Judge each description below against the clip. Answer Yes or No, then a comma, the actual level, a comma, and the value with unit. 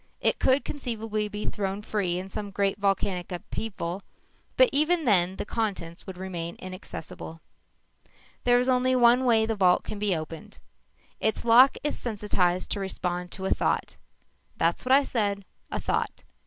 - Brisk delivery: No, average, 160 wpm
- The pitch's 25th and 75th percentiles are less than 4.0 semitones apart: No, average, 4.3 semitones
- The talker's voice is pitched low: No, high, 205 Hz